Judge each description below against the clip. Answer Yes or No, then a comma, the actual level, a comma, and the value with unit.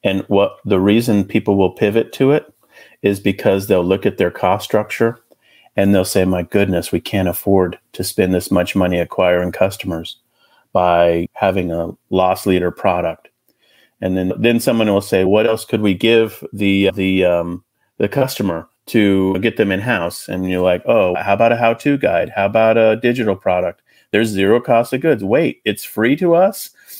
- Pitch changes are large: No, average, 3.4 semitones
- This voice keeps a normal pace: Yes, average, 185 wpm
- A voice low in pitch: Yes, low, 100 Hz